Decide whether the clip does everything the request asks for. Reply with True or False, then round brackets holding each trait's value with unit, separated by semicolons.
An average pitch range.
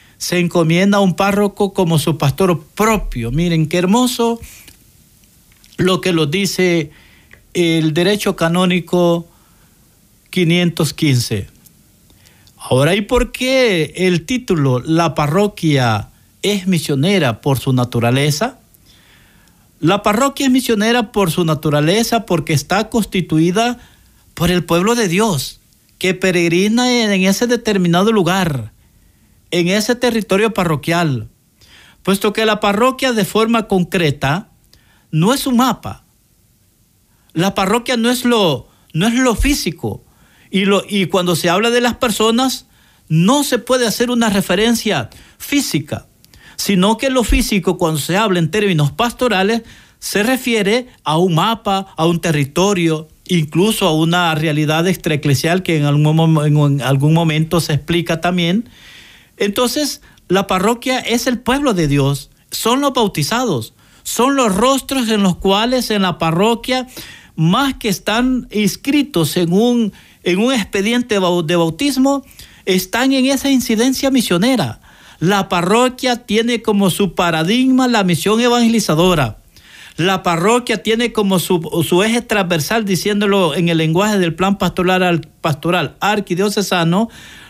False (5.8 semitones)